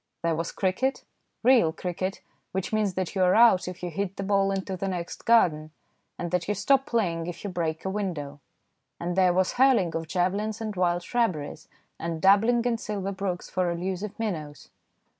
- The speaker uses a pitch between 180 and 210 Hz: Yes, medium, 185 Hz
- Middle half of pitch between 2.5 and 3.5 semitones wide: Yes, average, 3.2 semitones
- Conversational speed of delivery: Yes, average, 185 wpm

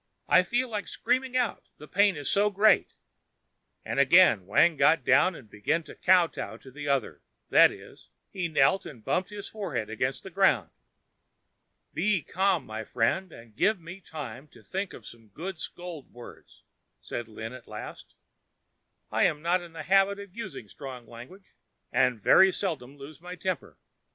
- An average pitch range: No, wide, 7.2 semitones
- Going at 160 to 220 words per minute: Yes, average, 170 wpm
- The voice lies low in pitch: No, medium, 165 Hz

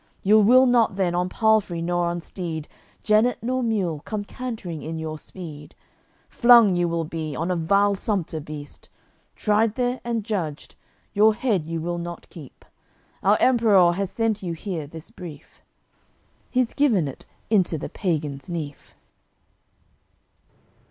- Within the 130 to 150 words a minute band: Yes, average, 145 wpm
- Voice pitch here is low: No, medium, 185 Hz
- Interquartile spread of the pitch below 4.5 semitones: No, average, 5.0 semitones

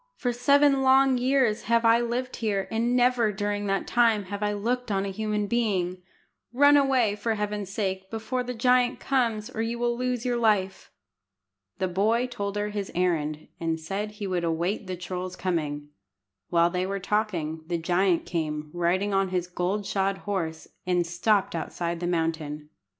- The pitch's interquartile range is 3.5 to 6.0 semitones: Yes, average, 4.6 semitones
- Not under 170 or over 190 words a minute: Yes, average, 175 wpm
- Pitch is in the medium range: No, high, 205 Hz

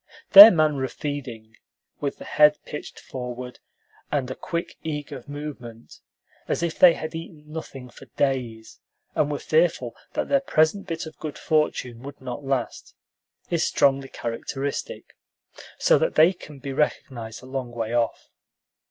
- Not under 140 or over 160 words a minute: Yes, average, 150 wpm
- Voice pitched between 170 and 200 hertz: No, medium, 140 Hz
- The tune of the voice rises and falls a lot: No, average, 3.7 semitones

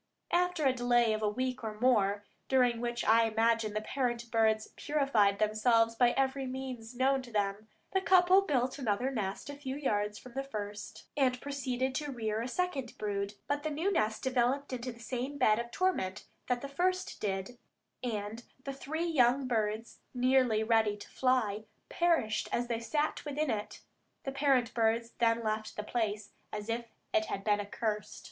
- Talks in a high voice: Yes, high, 240 Hz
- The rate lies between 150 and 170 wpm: No, average, 180 wpm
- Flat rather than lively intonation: No, average, 3.7 semitones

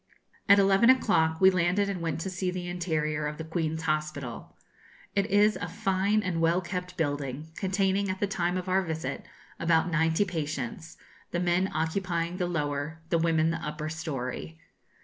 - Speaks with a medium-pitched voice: Yes, medium, 170 Hz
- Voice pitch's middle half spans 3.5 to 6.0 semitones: No, average, 3.1 semitones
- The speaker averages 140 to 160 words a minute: No, average, 170 wpm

